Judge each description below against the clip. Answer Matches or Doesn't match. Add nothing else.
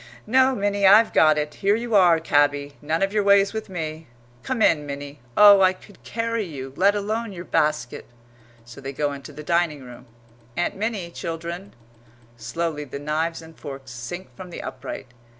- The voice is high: Doesn't match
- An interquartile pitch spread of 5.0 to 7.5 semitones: Matches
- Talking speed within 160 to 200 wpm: Matches